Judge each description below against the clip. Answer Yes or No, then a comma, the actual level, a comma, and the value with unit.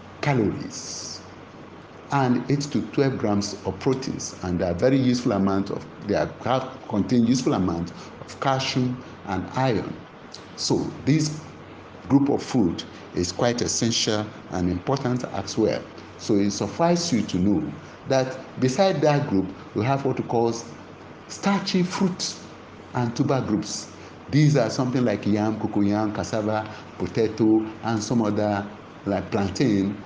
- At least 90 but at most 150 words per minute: Yes, slow, 135 wpm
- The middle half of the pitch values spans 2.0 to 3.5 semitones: No, average, 4.8 semitones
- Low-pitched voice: Yes, low, 110 Hz